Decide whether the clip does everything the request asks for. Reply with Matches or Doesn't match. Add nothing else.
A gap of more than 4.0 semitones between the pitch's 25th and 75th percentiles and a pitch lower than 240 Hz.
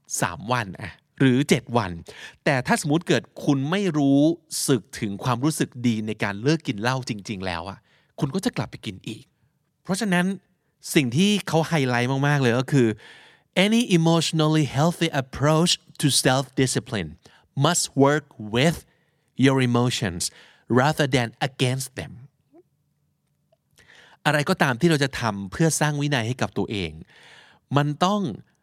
Matches